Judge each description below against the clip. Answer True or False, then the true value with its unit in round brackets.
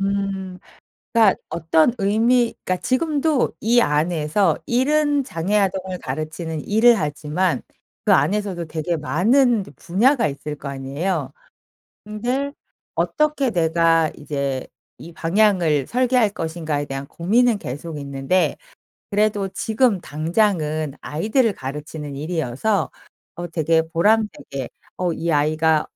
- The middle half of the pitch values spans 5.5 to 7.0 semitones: True (6.0 semitones)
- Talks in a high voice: False (175 Hz)